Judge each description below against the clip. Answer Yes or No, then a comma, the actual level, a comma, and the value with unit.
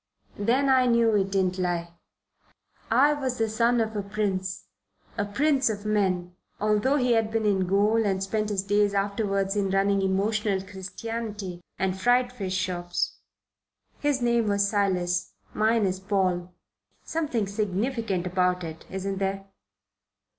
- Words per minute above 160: No, average, 145 wpm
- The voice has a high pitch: Yes, high, 205 Hz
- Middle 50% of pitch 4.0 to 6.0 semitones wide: No, average, 3.0 semitones